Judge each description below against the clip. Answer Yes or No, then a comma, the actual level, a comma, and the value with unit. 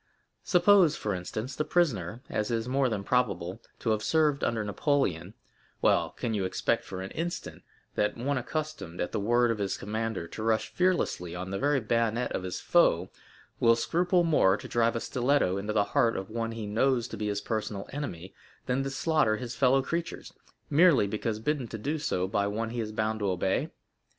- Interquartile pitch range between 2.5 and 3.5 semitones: No, average, 5.1 semitones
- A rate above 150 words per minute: Yes, average, 195 wpm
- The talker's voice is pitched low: Yes, low, 115 Hz